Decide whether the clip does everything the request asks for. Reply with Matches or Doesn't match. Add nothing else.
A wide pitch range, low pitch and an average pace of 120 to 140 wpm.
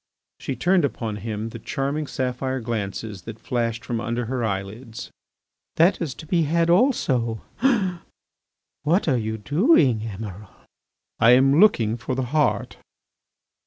Doesn't match